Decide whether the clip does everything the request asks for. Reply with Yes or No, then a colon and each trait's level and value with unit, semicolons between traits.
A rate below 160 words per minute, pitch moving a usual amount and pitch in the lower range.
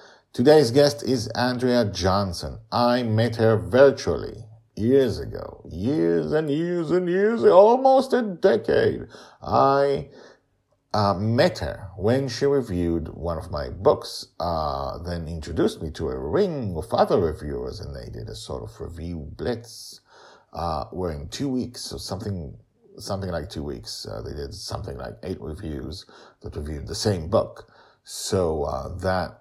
No: average, 150 wpm; wide, 7.8 semitones; low, 110 Hz